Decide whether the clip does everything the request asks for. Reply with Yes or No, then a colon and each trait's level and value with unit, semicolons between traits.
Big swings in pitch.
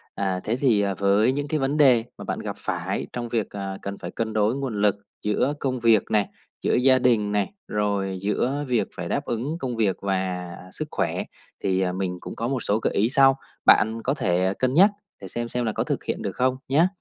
No: average, 4.6 semitones